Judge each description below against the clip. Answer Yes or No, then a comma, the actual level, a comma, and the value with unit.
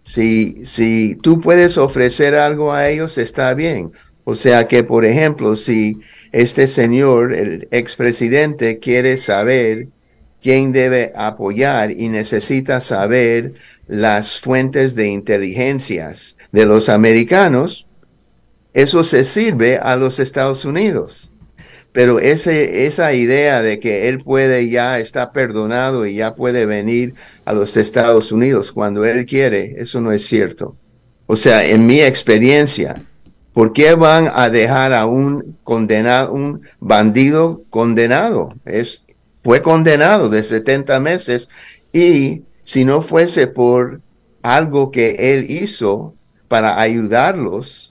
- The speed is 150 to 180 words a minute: No, slow, 125 wpm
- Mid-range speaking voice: No, low, 125 Hz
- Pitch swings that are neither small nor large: Yes, average, 3.3 semitones